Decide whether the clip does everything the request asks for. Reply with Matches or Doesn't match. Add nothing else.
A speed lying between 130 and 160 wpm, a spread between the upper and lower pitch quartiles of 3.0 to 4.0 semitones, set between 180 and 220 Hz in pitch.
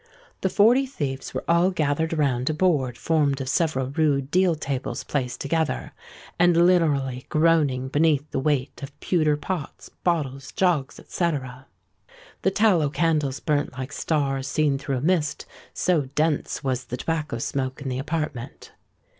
Doesn't match